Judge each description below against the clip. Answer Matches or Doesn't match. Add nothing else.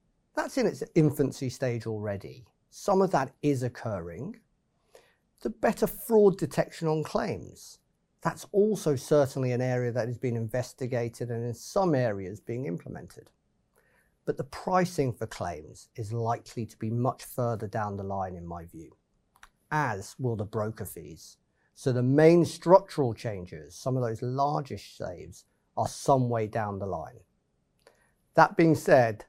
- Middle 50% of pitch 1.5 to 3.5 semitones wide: Doesn't match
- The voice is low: Matches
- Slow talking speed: Doesn't match